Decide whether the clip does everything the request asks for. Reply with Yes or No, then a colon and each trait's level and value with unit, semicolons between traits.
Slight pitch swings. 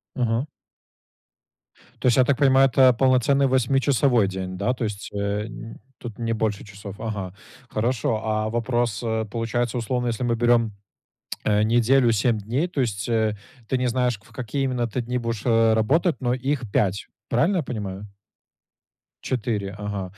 No: average, 3.1 semitones